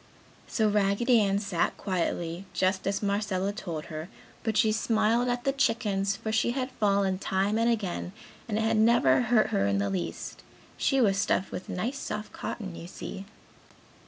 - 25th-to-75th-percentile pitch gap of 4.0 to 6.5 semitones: No, average, 3.0 semitones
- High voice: Yes, high, 205 Hz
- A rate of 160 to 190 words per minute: Yes, average, 175 wpm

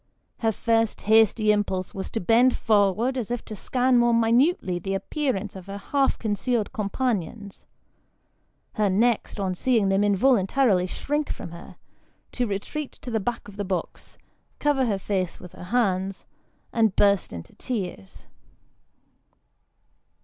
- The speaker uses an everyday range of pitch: Yes, average, 4.0 semitones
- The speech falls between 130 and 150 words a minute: Yes, average, 145 wpm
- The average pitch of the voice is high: Yes, high, 215 Hz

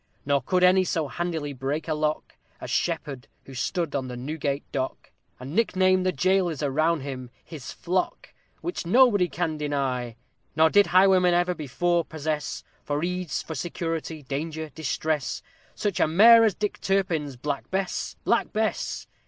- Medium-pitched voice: Yes, medium, 160 Hz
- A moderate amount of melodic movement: Yes, average, 4.1 semitones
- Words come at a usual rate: Yes, average, 160 wpm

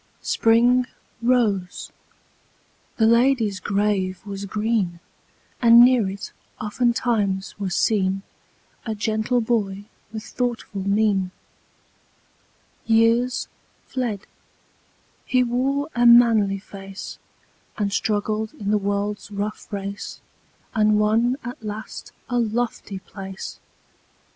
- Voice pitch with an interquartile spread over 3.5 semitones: No, average, 3.0 semitones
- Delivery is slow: Yes, slow, 100 wpm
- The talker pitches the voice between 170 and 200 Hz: No, high, 215 Hz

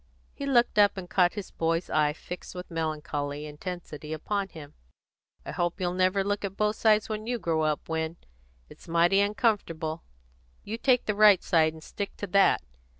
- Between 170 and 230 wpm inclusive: Yes, average, 180 wpm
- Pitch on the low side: No, medium, 180 Hz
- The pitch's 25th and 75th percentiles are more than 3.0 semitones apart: Yes, average, 4.4 semitones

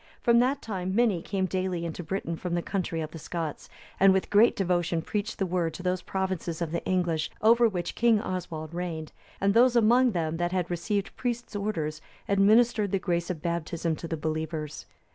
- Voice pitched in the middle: Yes, medium, 180 Hz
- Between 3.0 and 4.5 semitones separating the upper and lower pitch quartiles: Yes, average, 3.5 semitones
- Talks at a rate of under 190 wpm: No, average, 195 wpm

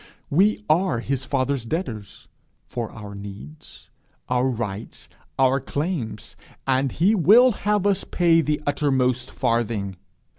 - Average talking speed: No, slow, 120 wpm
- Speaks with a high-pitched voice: No, low, 135 Hz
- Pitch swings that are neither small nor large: No, wide, 6.3 semitones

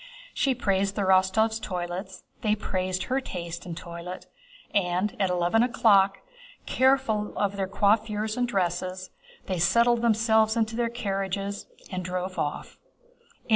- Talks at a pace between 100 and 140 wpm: Yes, slow, 135 wpm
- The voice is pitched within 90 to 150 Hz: No, high, 200 Hz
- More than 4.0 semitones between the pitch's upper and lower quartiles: No, average, 3.3 semitones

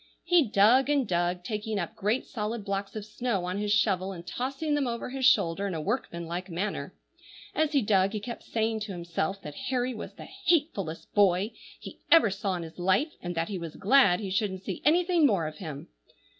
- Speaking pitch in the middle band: No, high, 205 Hz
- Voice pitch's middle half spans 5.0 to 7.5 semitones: Yes, wide, 5.6 semitones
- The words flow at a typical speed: No, fast, 210 wpm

